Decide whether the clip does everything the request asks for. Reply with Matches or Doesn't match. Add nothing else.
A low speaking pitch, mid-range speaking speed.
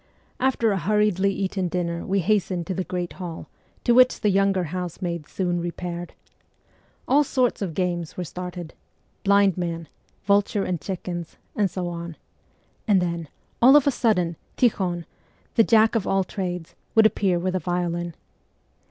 Doesn't match